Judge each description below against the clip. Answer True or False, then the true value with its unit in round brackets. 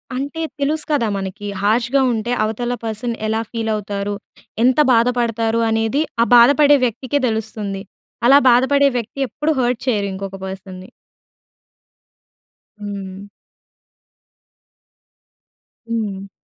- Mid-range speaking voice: False (225 Hz)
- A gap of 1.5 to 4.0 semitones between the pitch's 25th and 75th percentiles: True (3.4 semitones)